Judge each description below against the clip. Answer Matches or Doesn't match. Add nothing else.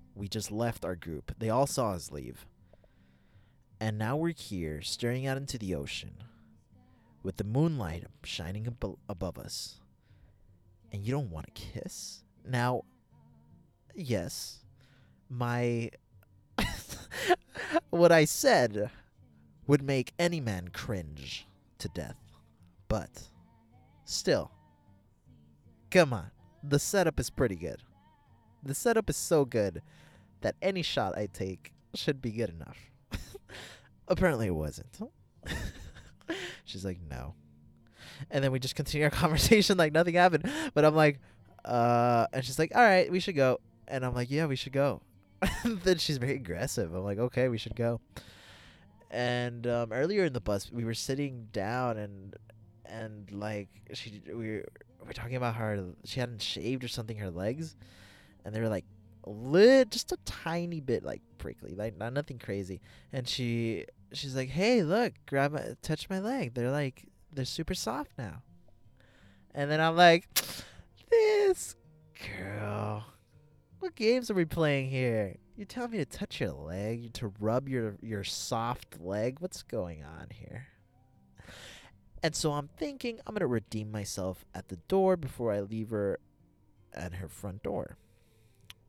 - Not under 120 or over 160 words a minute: Matches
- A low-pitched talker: Matches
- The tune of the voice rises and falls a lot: Matches